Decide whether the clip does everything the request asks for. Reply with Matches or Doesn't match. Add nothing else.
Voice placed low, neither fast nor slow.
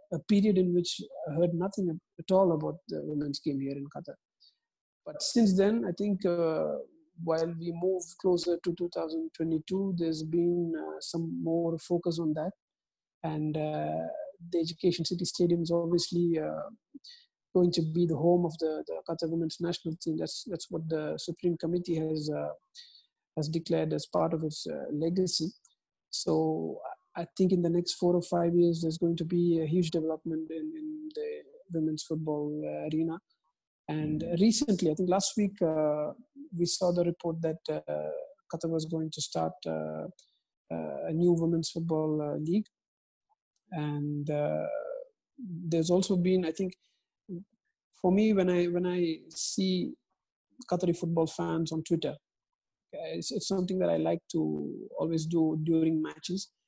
Doesn't match